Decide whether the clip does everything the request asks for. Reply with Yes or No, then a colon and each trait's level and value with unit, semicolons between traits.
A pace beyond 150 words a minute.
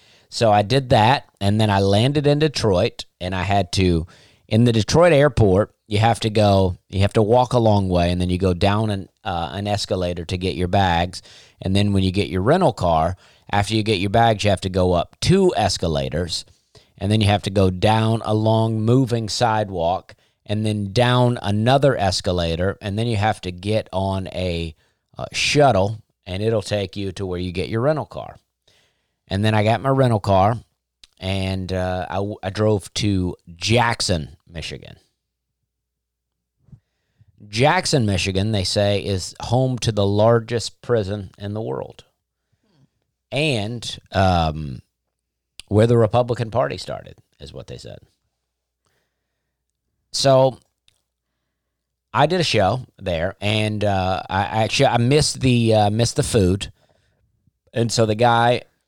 Yes: average, 160 wpm